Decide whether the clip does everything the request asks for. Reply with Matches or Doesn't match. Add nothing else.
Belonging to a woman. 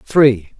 Doesn't match